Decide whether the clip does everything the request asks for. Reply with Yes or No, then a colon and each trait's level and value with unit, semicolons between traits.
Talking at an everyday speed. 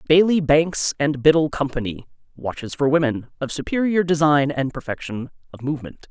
Yes: average, 145 wpm